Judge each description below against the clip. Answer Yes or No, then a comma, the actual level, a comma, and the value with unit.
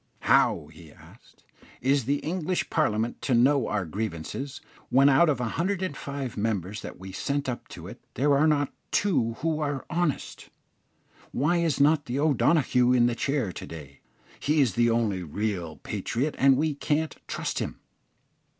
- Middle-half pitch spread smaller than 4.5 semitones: No, average, 5.1 semitones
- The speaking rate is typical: Yes, average, 160 wpm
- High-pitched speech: No, low, 135 Hz